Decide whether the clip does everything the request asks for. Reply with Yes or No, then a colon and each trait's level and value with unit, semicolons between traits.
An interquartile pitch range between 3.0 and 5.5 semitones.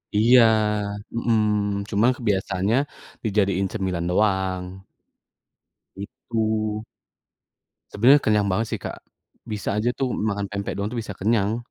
No: narrow, 2.5 semitones